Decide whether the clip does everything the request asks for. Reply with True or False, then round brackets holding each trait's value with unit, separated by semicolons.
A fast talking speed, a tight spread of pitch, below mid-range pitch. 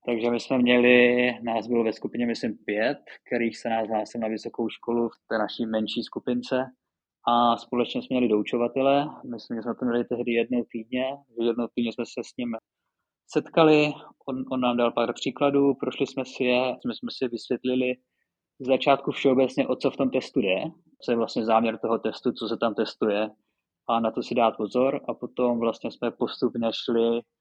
True (190 wpm; 1.9 semitones; 120 Hz)